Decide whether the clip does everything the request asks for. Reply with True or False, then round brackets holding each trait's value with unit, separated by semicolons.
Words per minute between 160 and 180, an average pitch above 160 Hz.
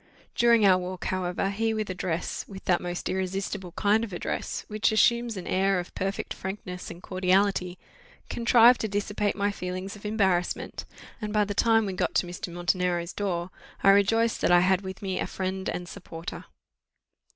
True (175 wpm; 190 Hz)